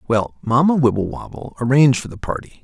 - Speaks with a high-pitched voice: No, low, 120 Hz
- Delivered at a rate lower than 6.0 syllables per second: No, 6.2 syllables/s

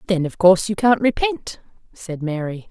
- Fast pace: No, average, 180 wpm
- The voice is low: No, medium, 185 Hz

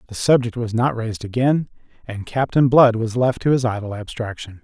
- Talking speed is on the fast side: No, average, 195 wpm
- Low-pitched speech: Yes, low, 115 Hz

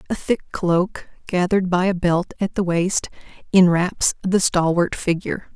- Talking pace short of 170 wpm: Yes, average, 150 wpm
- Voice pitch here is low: No, medium, 180 Hz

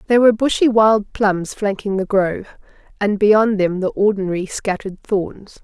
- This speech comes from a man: No, female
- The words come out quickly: No, average, 160 wpm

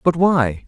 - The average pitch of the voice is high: No, medium, 150 Hz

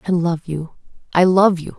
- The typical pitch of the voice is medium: Yes, medium, 175 Hz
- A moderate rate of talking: Yes, average, 170 wpm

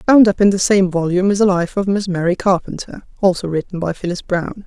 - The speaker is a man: No, female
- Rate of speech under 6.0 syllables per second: No, 6.2 syllables/s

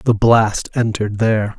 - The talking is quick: No, average, 150 wpm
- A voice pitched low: Yes, low, 110 Hz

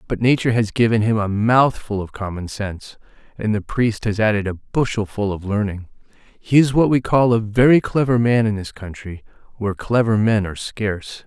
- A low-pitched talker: Yes, low, 110 Hz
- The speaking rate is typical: Yes, average, 190 wpm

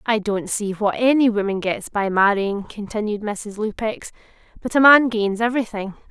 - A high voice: Yes, high, 215 Hz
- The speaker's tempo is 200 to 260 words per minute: No, average, 165 wpm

